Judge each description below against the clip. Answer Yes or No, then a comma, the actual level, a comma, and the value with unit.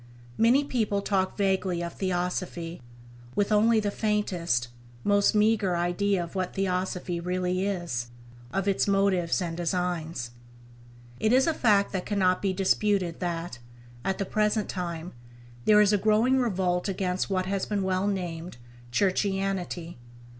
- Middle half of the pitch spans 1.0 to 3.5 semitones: Yes, narrow, 2.5 semitones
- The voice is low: No, high, 190 Hz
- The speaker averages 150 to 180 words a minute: No, average, 140 wpm